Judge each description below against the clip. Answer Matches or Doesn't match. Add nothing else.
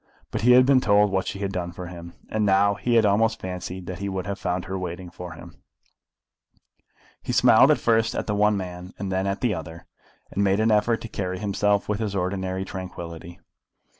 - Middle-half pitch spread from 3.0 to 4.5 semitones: Doesn't match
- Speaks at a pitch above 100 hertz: Doesn't match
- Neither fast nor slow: Doesn't match